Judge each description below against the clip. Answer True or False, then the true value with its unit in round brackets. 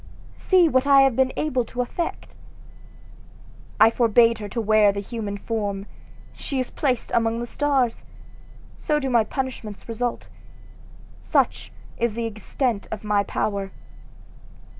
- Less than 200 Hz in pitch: False (230 Hz)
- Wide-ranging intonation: False (3.4 semitones)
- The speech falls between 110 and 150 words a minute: True (140 wpm)